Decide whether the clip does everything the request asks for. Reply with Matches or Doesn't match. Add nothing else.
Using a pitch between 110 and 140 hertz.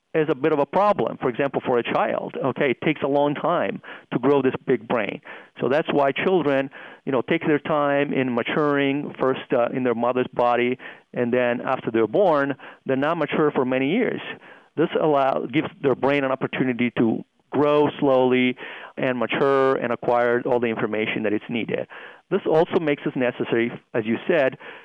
Matches